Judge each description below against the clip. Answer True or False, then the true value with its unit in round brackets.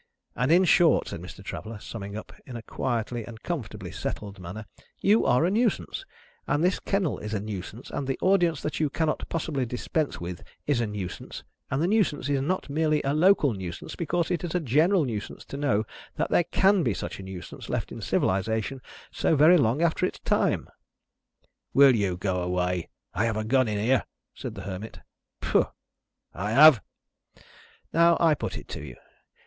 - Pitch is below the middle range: True (130 Hz)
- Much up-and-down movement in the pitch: True (7.6 semitones)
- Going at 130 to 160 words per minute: False (185 wpm)